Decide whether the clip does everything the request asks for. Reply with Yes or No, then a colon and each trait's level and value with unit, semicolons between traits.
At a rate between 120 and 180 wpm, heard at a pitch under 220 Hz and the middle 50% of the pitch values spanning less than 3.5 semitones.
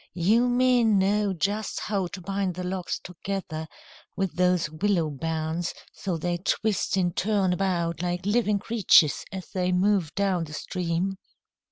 Yes: average, 150 wpm; medium, 185 Hz; narrow, 2.6 semitones